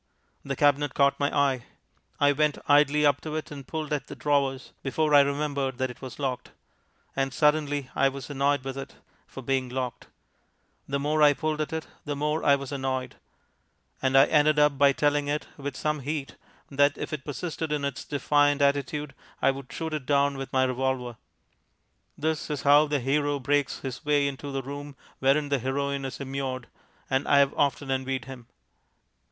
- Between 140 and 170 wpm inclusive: No, average, 190 wpm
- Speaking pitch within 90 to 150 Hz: Yes, medium, 140 Hz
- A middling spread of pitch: No, narrow, 1.6 semitones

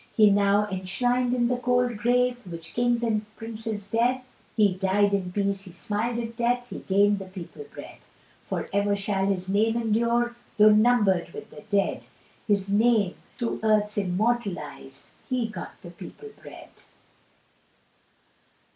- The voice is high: Yes, high, 210 Hz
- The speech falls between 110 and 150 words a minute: Yes, average, 145 wpm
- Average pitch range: Yes, average, 3.3 semitones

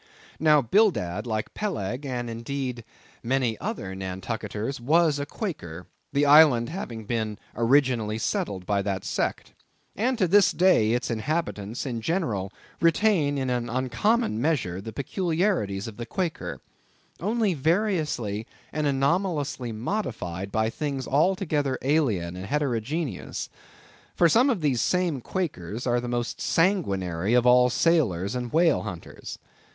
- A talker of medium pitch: No, low, 130 Hz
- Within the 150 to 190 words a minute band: No, slow, 135 wpm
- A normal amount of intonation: No, wide, 6.9 semitones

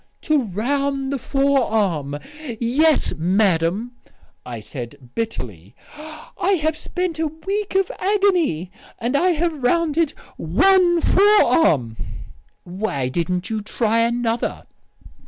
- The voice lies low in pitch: No, very high, 250 Hz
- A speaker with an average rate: No, slow, 105 wpm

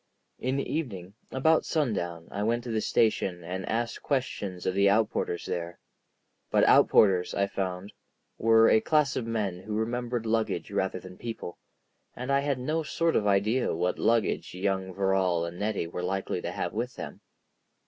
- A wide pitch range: No, average, 4.5 semitones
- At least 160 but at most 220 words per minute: Yes, average, 170 wpm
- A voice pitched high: No, low, 105 Hz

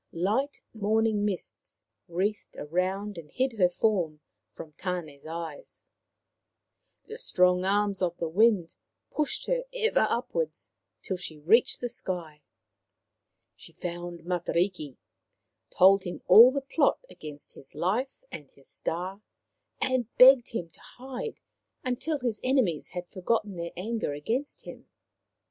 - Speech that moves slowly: Yes, slow, 130 wpm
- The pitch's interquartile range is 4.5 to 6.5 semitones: Yes, wide, 5.6 semitones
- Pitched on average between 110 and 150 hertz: No, high, 190 Hz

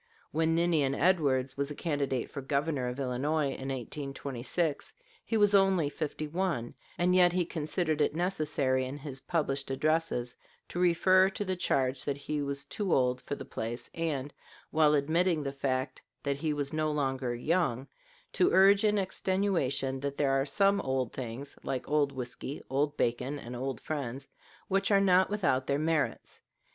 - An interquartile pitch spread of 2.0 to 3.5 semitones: No, average, 4.2 semitones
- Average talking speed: Yes, average, 170 wpm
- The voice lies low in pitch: No, medium, 145 Hz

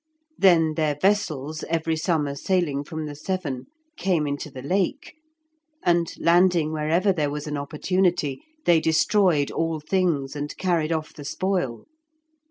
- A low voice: No, medium, 160 Hz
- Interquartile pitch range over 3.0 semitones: Yes, average, 3.5 semitones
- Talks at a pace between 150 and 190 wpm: No, average, 140 wpm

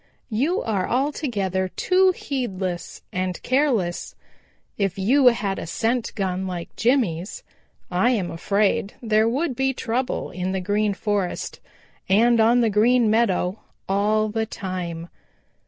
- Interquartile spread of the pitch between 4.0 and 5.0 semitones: Yes, average, 4.4 semitones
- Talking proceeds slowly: Yes, slow, 130 wpm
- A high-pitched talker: Yes, high, 215 Hz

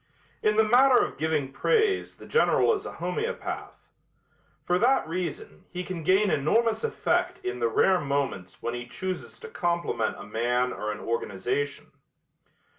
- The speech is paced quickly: No, average, 155 wpm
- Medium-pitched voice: Yes, medium, 170 Hz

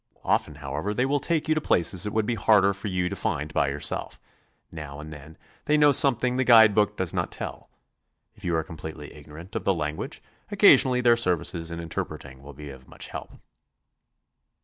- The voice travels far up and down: Yes, wide, 7.2 semitones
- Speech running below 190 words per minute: No, average, 195 wpm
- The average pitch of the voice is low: Yes, very low, 90 Hz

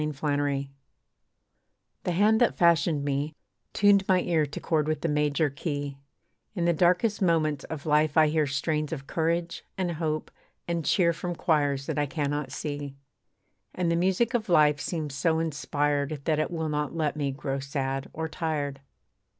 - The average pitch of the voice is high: No, medium, 155 Hz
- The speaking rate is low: No, average, 170 wpm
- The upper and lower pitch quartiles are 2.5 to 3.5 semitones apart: Yes, average, 2.8 semitones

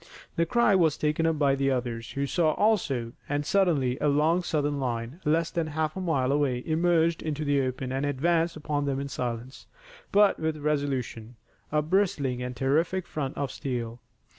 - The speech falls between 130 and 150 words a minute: No, average, 175 wpm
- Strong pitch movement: No, average, 3.7 semitones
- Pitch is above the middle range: No, medium, 145 Hz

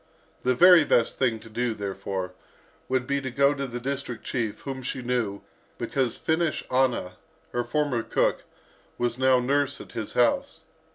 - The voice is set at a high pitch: No, low, 125 Hz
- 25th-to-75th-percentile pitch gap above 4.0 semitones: No, average, 3.0 semitones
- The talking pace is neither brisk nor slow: Yes, average, 165 wpm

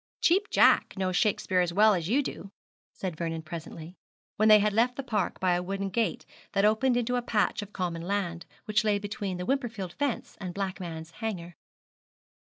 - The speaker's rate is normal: Yes, average, 185 wpm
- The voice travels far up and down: No, average, 3.8 semitones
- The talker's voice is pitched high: Yes, high, 200 Hz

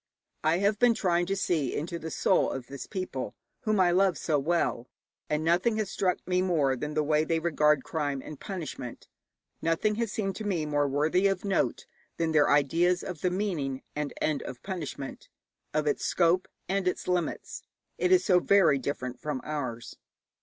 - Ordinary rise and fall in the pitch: Yes, average, 4.2 semitones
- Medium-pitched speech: Yes, medium, 165 Hz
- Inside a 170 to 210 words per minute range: Yes, average, 185 wpm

